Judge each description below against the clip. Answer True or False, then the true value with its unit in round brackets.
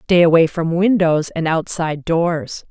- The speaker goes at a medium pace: True (155 wpm)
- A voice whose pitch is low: False (165 Hz)